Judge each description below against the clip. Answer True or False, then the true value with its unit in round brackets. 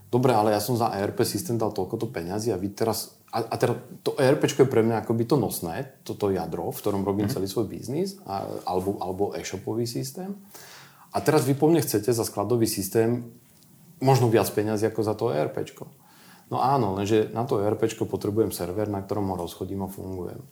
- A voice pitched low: True (110 Hz)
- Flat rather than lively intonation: False (4.3 semitones)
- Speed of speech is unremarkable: False (195 wpm)